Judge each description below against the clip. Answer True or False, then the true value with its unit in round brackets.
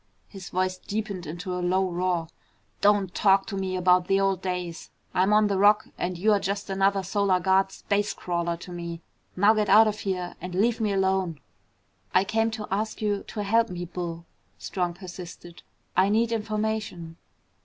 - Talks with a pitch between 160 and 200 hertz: True (190 Hz)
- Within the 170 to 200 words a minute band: True (175 wpm)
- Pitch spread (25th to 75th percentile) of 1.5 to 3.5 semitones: True (2.5 semitones)